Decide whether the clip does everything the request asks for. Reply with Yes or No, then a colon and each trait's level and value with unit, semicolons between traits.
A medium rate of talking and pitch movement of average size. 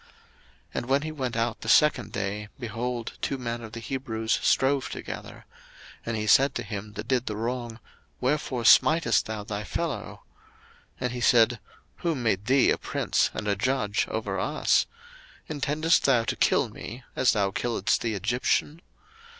Yes: average, 170 wpm; average, 3.5 semitones